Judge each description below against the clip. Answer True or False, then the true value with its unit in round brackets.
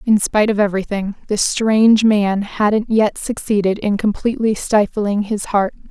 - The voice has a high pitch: True (210 Hz)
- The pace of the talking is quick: False (150 wpm)